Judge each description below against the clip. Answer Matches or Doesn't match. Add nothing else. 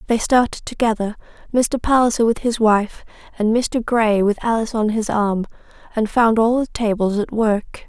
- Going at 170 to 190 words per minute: Matches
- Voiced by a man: Doesn't match